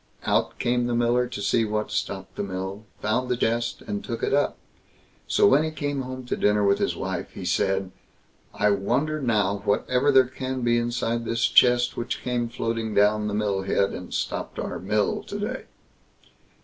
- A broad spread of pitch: No, average, 3.5 semitones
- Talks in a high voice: No, low, 120 Hz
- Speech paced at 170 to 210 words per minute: Yes, average, 190 wpm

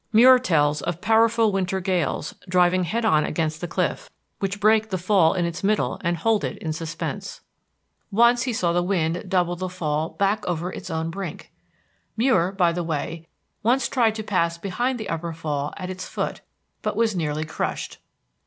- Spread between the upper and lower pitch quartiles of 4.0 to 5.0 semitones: Yes, average, 4.5 semitones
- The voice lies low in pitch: No, medium, 180 Hz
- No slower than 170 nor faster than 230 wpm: Yes, average, 180 wpm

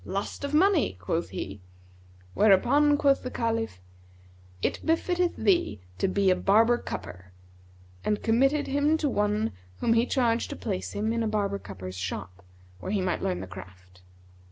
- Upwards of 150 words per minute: Yes, average, 160 wpm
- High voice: Yes, high, 205 Hz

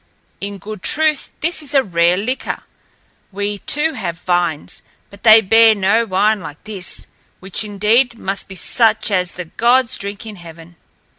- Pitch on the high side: Yes, high, 205 Hz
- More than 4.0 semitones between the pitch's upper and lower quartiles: No, average, 3.7 semitones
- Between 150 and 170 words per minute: Yes, average, 160 wpm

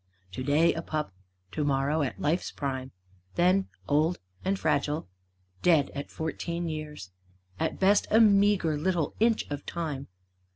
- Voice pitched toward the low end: No, medium, 155 Hz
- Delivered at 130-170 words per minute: Yes, slow, 135 wpm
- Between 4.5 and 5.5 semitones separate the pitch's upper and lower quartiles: No, average, 3.8 semitones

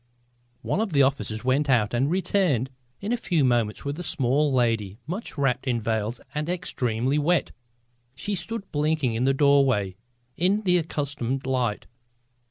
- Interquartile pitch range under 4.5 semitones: No, average, 5.2 semitones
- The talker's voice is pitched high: No, low, 135 Hz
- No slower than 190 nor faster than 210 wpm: No, average, 160 wpm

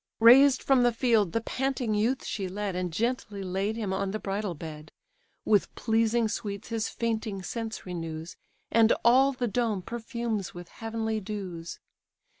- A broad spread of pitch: No, average, 3.4 semitones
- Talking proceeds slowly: No, average, 155 wpm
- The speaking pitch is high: Yes, high, 220 Hz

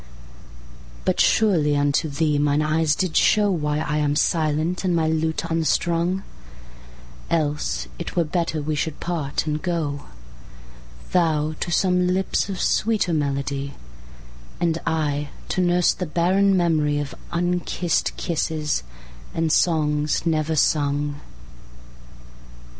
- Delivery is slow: Yes, slow, 110 wpm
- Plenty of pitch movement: No, average, 2.9 semitones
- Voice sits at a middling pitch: Yes, medium, 155 Hz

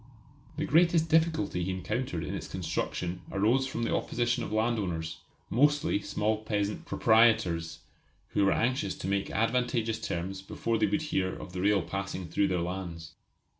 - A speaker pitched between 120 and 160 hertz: No, low, 105 Hz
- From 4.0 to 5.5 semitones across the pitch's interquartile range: Yes, average, 4.4 semitones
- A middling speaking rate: Yes, average, 160 wpm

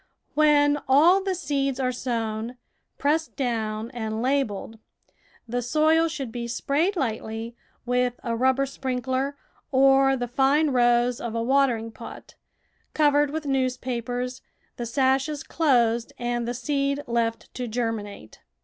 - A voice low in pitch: No, very high, 255 Hz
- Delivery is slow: Yes, slow, 130 wpm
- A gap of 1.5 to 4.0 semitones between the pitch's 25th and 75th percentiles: Yes, average, 2.9 semitones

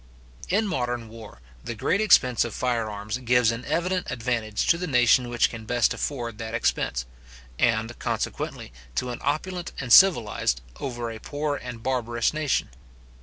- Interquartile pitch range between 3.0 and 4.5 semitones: Yes, average, 3.8 semitones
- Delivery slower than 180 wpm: Yes, average, 155 wpm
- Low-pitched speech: Yes, low, 120 Hz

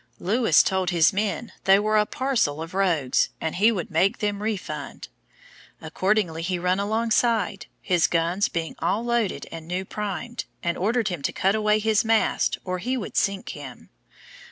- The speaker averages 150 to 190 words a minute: Yes, average, 170 wpm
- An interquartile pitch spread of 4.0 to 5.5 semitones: No, average, 3.6 semitones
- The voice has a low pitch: No, high, 195 Hz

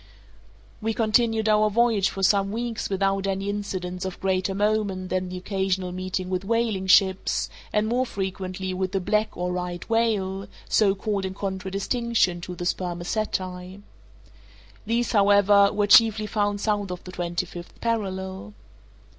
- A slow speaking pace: No, average, 145 wpm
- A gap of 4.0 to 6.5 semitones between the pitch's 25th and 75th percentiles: No, narrow, 2.4 semitones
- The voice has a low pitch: No, high, 195 Hz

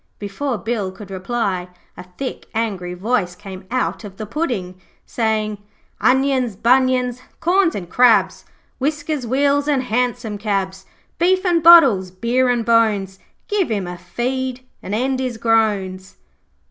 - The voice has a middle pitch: No, high, 230 Hz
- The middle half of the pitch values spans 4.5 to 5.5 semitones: Yes, average, 5.0 semitones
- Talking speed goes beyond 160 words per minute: No, slow, 135 wpm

